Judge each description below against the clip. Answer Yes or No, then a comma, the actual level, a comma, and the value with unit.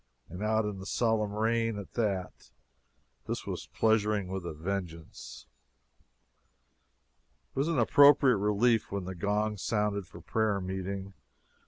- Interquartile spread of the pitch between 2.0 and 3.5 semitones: Yes, average, 2.7 semitones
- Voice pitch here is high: No, low, 105 Hz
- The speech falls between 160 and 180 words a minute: No, slow, 135 wpm